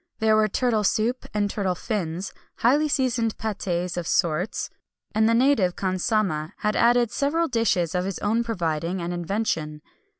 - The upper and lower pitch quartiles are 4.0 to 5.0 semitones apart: Yes, average, 4.6 semitones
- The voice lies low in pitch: No, high, 210 Hz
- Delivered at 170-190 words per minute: No, average, 155 wpm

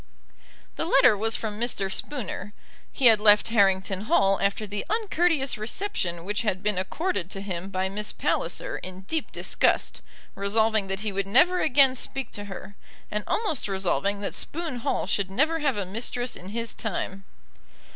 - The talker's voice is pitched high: Yes, high, 210 Hz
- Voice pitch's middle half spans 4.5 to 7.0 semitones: Yes, average, 5.0 semitones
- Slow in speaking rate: No, average, 165 wpm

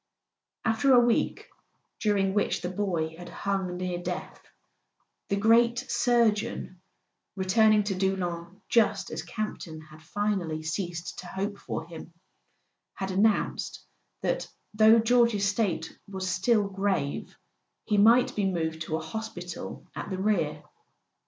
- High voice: Yes, high, 195 Hz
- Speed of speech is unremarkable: No, slow, 125 wpm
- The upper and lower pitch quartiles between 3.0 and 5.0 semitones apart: Yes, average, 3.5 semitones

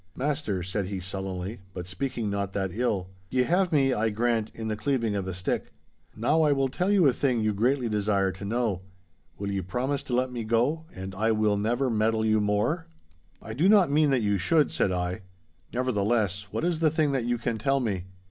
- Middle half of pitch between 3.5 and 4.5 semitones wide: No, average, 5.2 semitones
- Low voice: Yes, low, 115 Hz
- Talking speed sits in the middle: No, fast, 215 wpm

